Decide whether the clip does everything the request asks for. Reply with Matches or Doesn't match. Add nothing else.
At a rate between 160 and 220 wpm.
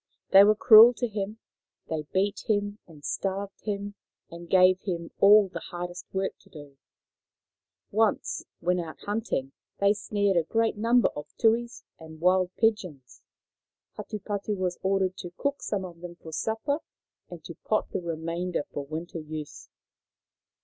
Doesn't match